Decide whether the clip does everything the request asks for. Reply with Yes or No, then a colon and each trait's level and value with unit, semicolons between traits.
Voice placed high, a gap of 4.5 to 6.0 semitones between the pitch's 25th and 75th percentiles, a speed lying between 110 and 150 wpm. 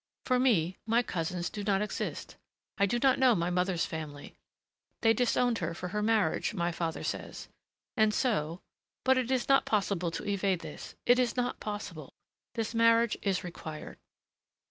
No: high, 205 Hz; average, 5.2 semitones; average, 165 wpm